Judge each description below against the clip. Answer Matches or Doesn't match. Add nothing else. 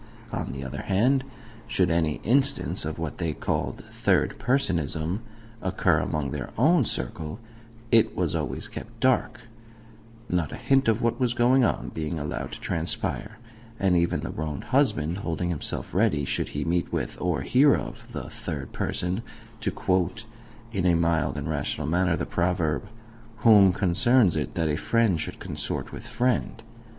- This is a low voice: Matches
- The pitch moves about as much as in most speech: Doesn't match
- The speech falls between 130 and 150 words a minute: Doesn't match